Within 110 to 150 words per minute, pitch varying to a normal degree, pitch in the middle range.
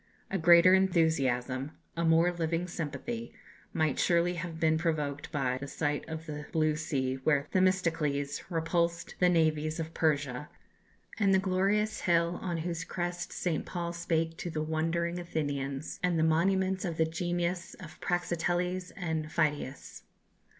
No: average, 145 wpm; narrow, 2.3 semitones; medium, 165 Hz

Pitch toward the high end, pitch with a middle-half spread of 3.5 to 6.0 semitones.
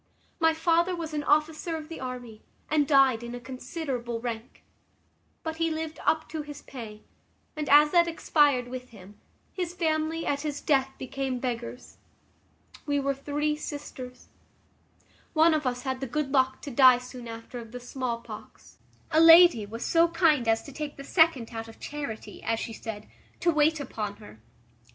Yes: very high, 275 Hz; average, 4.4 semitones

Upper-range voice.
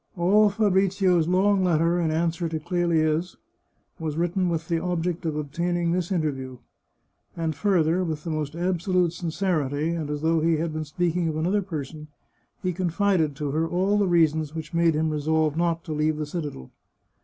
No: medium, 165 Hz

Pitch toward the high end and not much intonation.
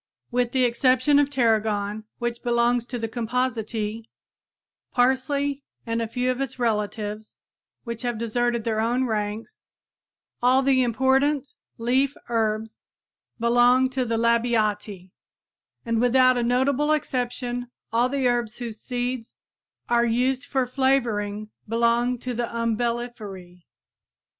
Yes: high, 240 Hz; narrow, 2.1 semitones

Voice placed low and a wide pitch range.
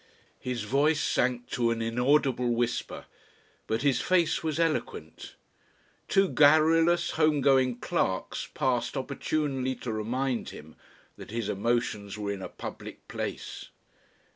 No: low, 130 Hz; average, 4.3 semitones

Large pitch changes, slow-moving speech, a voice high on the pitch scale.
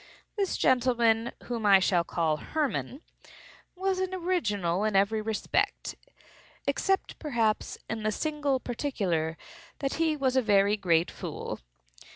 Yes: wide, 6.7 semitones; slow, 125 wpm; high, 230 Hz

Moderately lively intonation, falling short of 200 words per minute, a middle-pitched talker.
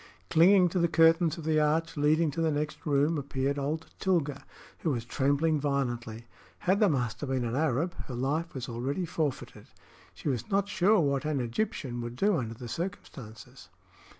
Yes: average, 4.3 semitones; average, 180 wpm; medium, 145 Hz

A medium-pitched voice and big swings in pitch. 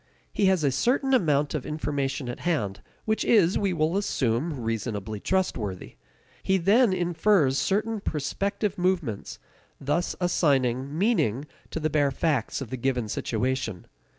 Yes: medium, 150 Hz; wide, 6.6 semitones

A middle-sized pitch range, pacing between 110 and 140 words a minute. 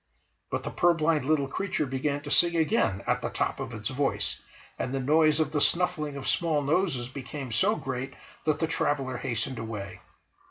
No: average, 3.6 semitones; average, 185 wpm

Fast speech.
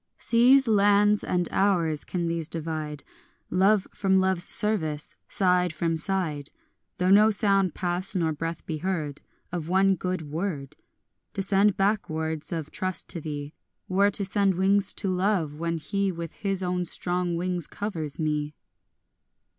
No: average, 155 wpm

